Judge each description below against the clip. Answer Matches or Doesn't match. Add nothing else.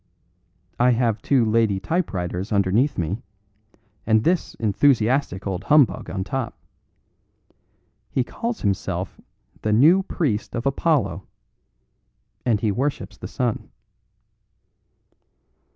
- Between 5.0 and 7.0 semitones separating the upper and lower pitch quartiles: Matches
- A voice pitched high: Doesn't match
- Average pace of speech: Doesn't match